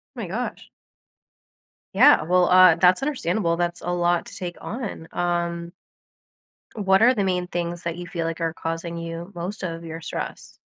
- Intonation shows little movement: Yes, narrow, 1.5 semitones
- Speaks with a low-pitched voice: No, medium, 175 Hz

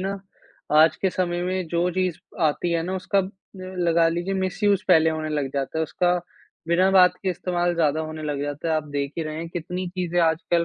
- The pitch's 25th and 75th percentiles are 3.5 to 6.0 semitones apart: No, narrow, 2.6 semitones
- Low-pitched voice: No, medium, 175 Hz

